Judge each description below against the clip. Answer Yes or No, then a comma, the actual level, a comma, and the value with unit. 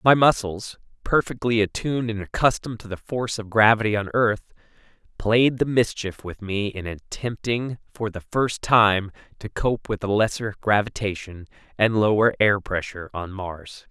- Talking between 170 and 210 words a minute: No, average, 155 wpm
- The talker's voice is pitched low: Yes, low, 105 Hz